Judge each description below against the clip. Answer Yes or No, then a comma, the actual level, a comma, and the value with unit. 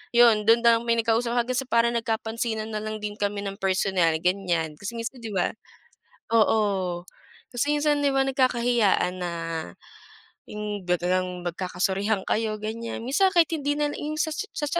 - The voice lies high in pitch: Yes, high, 220 Hz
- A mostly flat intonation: No, average, 4.0 semitones